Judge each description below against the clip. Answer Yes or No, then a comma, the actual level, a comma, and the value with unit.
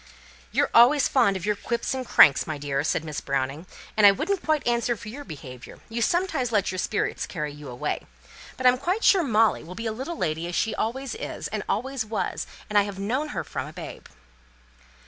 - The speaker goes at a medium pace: No, fast, 220 wpm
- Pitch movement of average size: No, wide, 7.9 semitones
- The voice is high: Yes, high, 220 Hz